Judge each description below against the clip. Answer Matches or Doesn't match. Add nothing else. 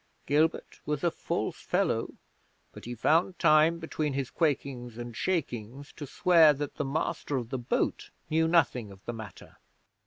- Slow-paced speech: Doesn't match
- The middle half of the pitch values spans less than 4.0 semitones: Doesn't match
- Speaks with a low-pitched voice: Doesn't match